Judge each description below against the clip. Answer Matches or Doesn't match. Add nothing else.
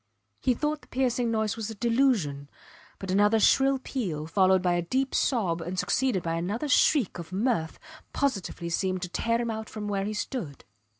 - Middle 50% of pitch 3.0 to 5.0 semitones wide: Doesn't match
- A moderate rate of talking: Matches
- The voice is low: Doesn't match